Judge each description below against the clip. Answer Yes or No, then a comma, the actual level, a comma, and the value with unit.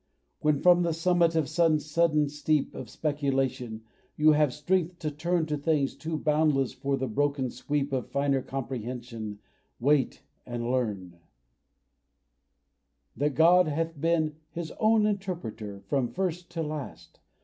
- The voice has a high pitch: No, medium, 150 Hz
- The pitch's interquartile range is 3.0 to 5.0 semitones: Yes, average, 3.7 semitones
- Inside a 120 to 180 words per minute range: Yes, average, 140 wpm